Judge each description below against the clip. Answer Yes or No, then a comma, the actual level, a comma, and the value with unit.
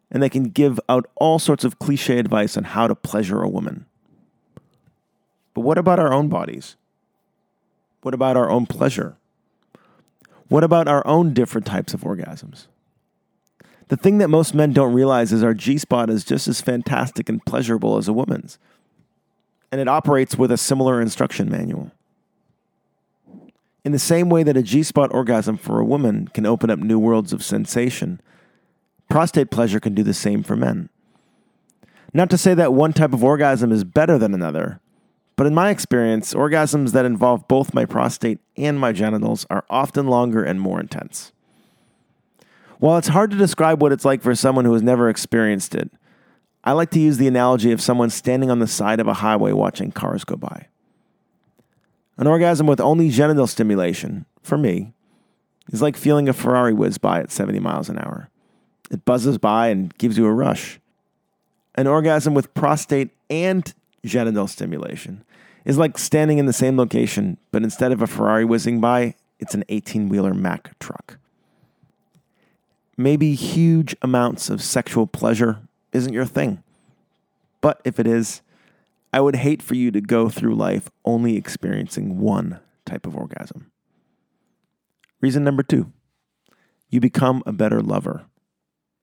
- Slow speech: No, average, 165 wpm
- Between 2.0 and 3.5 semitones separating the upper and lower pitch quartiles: No, average, 4.6 semitones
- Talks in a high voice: No, low, 130 Hz